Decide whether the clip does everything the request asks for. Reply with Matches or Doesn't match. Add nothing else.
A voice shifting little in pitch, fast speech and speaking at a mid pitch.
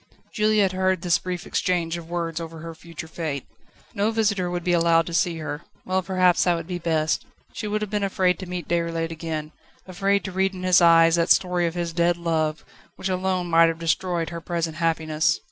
Matches